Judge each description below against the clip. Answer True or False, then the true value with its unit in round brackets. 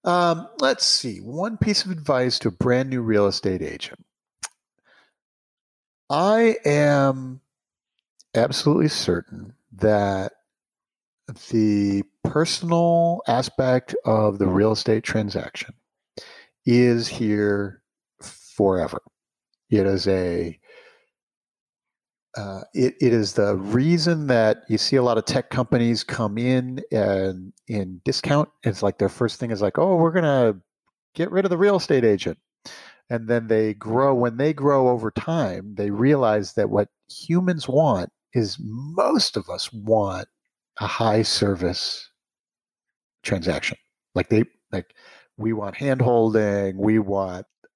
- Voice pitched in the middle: False (115 Hz)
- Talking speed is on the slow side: True (125 wpm)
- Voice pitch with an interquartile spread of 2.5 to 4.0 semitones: False (5.5 semitones)